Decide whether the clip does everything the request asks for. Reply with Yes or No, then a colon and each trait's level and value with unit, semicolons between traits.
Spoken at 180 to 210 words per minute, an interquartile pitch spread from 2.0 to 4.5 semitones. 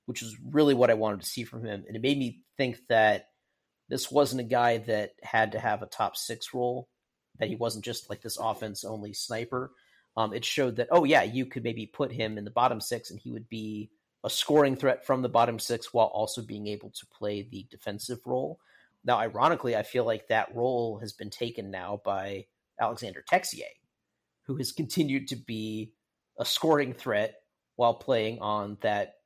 Yes: average, 200 wpm; average, 3.2 semitones